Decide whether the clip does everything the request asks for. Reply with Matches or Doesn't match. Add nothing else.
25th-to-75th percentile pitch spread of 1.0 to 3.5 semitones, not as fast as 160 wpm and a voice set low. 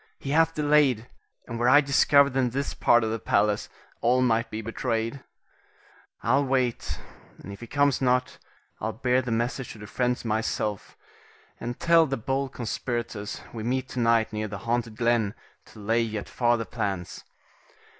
Doesn't match